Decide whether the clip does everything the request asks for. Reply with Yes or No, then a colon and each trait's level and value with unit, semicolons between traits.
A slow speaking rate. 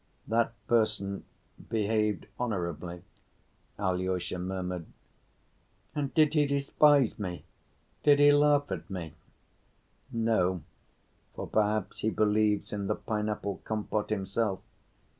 Yes: slow, 105 wpm